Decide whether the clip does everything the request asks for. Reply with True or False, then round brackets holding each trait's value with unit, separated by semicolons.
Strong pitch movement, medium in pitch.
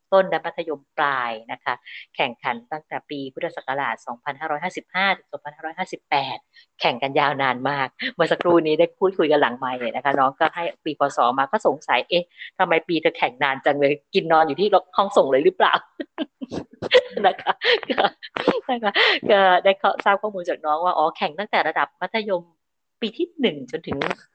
False (4.5 semitones; 175 Hz)